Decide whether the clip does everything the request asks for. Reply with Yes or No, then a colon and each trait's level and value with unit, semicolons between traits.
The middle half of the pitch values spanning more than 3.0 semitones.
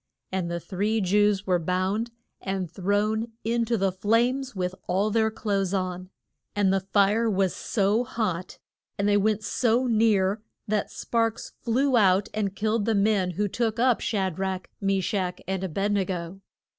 No: average, 2.7 semitones